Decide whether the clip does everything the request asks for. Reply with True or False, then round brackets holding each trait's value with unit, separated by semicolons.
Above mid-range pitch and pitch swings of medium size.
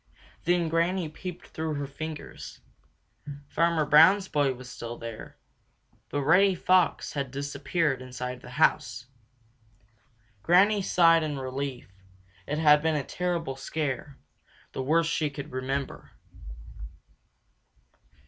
False (150 Hz; 3.7 semitones)